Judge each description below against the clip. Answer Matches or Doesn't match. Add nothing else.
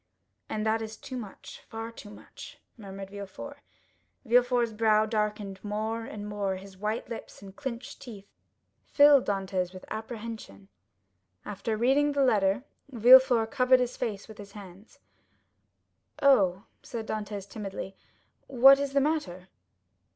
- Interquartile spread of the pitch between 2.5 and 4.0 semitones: Matches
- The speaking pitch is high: Matches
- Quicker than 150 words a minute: Doesn't match